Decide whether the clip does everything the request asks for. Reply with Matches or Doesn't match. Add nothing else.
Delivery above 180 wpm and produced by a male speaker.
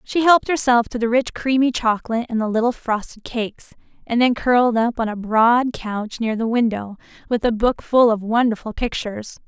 Doesn't match